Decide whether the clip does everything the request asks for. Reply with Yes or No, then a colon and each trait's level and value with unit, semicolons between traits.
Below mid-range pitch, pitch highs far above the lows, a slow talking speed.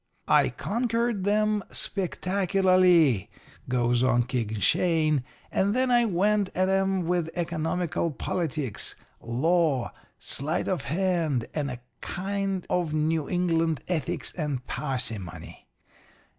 No: medium, 170 Hz; wide, 5.8 semitones; slow, 110 wpm